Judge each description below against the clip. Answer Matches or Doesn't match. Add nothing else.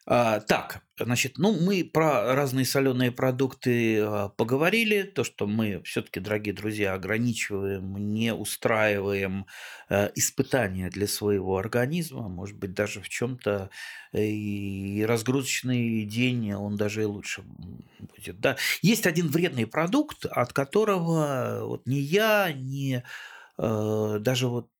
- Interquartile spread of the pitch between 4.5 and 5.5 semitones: Matches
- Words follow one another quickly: Doesn't match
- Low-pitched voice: Matches